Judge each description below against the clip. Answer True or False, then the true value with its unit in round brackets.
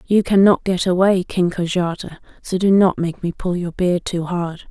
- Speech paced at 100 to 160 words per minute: False (205 wpm)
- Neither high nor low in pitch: True (180 Hz)